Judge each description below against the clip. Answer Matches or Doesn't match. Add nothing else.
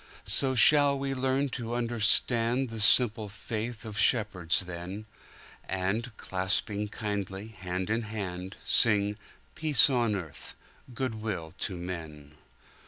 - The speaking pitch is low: Matches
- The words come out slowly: Matches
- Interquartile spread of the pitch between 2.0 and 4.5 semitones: Matches